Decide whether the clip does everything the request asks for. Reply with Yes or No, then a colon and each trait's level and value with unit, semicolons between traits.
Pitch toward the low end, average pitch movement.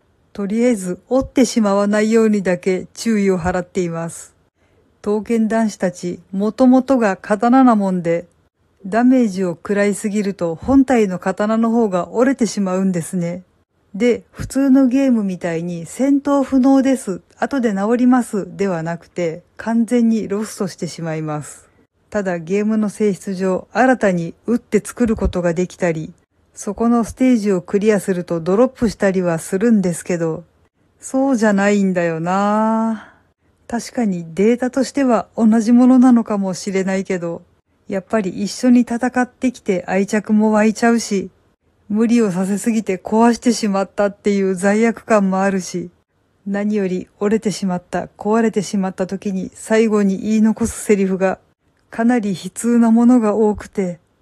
No: high, 205 Hz; average, 3.6 semitones